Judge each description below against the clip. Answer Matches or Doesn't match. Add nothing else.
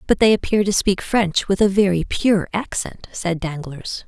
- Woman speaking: Matches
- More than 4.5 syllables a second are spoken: Doesn't match